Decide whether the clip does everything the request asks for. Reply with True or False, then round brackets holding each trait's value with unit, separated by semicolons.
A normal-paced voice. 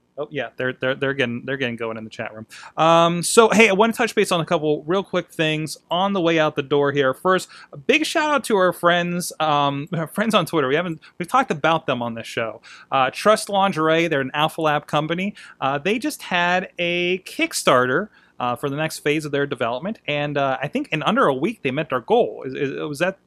False (245 wpm)